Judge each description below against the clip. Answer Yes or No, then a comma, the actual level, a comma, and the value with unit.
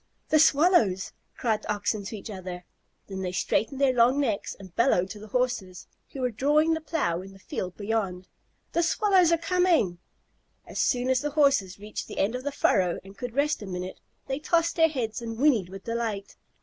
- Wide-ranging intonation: Yes, wide, 6.8 semitones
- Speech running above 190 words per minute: Yes, average, 200 wpm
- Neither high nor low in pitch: No, high, 230 Hz